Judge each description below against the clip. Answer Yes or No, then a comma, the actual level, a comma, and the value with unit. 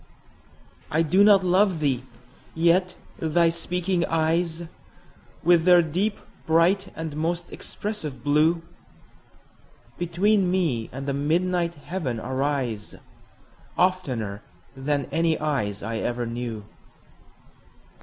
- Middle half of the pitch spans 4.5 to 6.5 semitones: Yes, average, 4.8 semitones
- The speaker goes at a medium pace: No, slow, 105 wpm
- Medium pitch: Yes, medium, 160 Hz